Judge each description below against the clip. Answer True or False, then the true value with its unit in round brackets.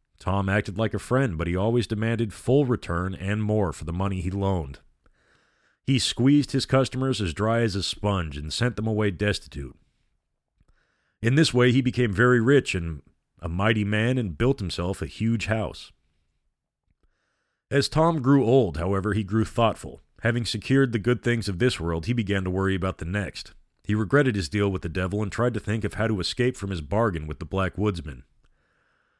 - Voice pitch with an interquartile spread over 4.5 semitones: True (5.2 semitones)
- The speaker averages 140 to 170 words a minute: False (195 wpm)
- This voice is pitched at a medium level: False (105 Hz)